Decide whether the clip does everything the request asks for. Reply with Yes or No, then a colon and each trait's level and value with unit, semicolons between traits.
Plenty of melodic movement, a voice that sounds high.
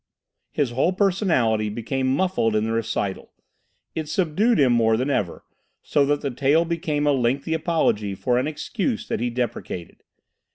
No: wide, 5.9 semitones; low, 135 Hz